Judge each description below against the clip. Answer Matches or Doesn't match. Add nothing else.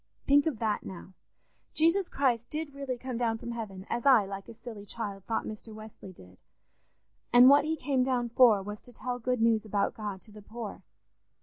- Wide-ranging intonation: Doesn't match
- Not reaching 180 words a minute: Doesn't match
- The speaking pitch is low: Doesn't match